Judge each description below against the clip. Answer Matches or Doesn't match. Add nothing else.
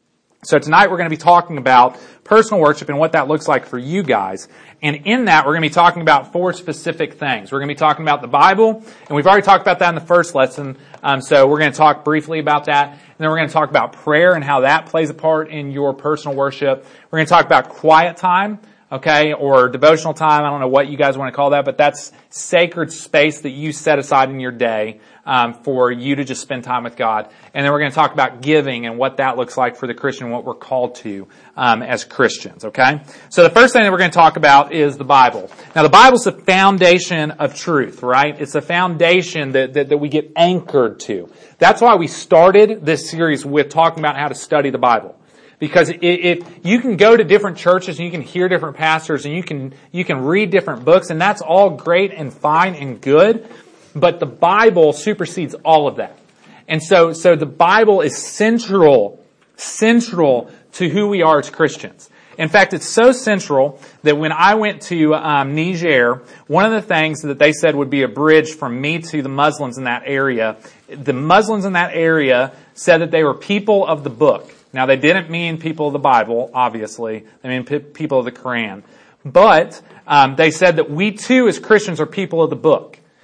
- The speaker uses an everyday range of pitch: Matches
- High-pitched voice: Doesn't match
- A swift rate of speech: Matches